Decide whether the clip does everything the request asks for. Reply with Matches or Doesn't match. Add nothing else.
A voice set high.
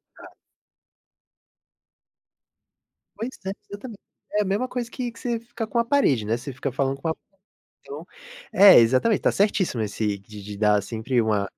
Doesn't match